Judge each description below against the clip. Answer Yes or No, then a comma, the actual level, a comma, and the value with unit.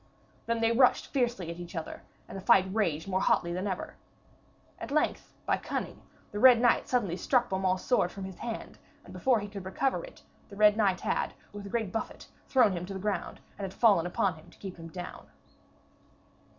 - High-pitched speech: Yes, high, 200 Hz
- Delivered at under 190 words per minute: No, fast, 205 wpm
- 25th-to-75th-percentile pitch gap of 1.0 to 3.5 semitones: No, average, 4.1 semitones